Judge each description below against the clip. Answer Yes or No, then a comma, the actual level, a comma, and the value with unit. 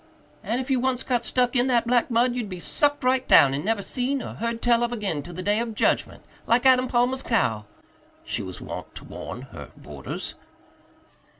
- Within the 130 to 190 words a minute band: No, fast, 205 wpm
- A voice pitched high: Yes, high, 240 Hz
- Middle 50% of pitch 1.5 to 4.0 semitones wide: Yes, average, 3.6 semitones